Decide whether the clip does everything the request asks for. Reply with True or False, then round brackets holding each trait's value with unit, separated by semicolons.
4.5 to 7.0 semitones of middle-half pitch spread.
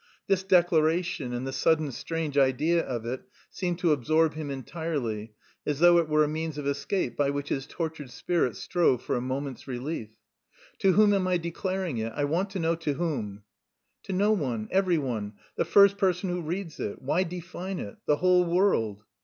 True (5.1 semitones)